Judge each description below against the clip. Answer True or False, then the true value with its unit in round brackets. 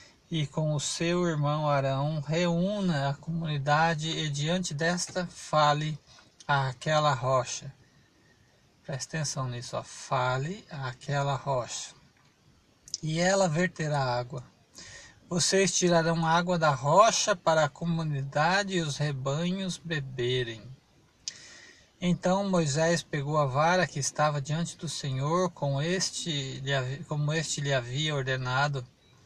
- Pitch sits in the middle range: True (150 Hz)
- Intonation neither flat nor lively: True (3.3 semitones)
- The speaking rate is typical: False (115 wpm)